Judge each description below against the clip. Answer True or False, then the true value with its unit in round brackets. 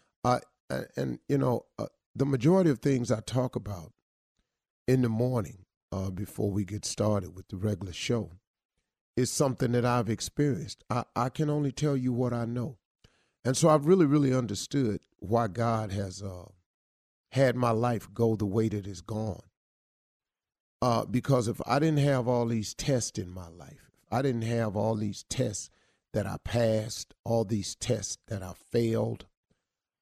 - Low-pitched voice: True (115 Hz)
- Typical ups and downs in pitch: True (3.9 semitones)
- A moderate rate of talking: True (170 wpm)